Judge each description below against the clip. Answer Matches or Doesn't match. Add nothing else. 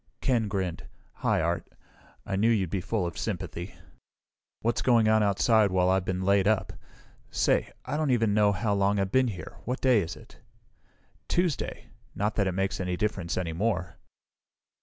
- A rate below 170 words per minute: Doesn't match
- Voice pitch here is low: Matches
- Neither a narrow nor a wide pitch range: Matches